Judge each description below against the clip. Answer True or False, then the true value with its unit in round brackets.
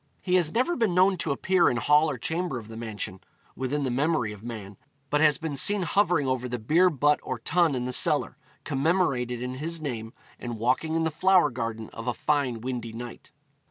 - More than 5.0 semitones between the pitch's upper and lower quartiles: True (5.4 semitones)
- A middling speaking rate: False (210 wpm)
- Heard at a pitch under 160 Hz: True (140 Hz)